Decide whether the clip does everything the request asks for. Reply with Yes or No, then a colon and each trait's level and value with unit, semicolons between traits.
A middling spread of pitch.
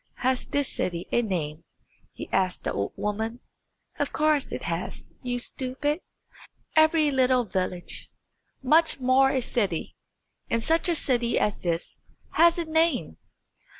No: wide, 6.6 semitones